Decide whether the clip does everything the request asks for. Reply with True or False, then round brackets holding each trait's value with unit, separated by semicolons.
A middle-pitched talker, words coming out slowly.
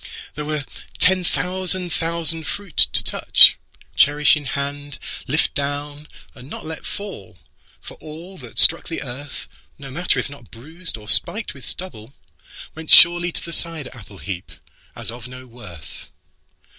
True (145 Hz; 130 wpm)